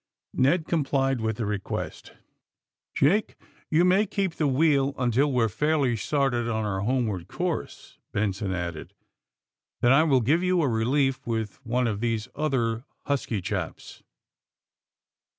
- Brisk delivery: No, average, 155 wpm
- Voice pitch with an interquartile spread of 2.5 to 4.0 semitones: No, average, 5.0 semitones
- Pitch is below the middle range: Yes, low, 130 Hz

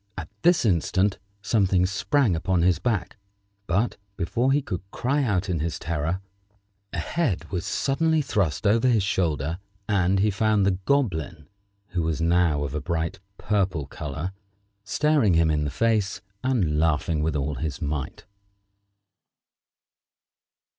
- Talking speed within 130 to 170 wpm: Yes, average, 140 wpm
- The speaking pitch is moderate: No, very low, 90 Hz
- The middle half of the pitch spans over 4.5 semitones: Yes, average, 5.0 semitones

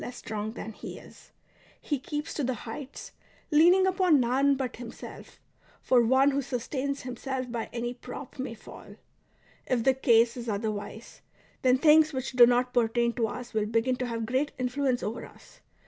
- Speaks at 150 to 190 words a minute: Yes, average, 180 wpm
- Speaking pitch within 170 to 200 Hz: No, very high, 250 Hz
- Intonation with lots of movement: No, average, 2.7 semitones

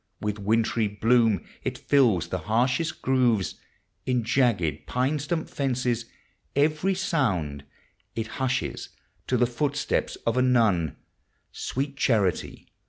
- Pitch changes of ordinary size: Yes, average, 4.1 semitones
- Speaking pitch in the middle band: No, low, 120 Hz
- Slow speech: Yes, slow, 120 wpm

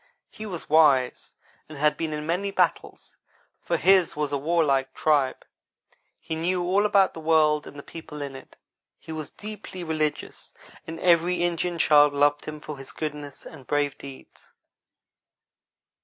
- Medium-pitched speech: Yes, medium, 155 Hz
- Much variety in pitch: No, average, 2.9 semitones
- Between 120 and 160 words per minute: Yes, average, 155 wpm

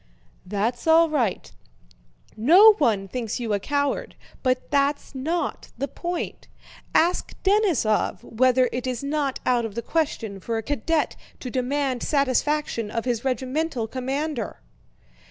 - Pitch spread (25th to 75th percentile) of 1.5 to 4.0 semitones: No, average, 4.5 semitones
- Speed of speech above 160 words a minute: No, slow, 135 wpm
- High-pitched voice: Yes, very high, 260 Hz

